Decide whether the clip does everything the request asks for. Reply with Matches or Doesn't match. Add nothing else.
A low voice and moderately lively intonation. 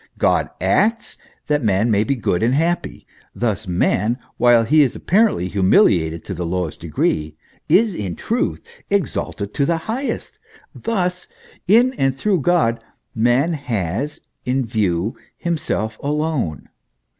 Doesn't match